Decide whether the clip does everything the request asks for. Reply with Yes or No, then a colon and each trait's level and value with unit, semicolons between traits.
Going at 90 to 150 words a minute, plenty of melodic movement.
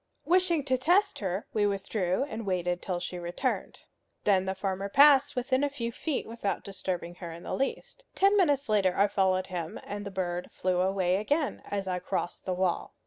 No: average, 195 wpm; wide, 6.3 semitones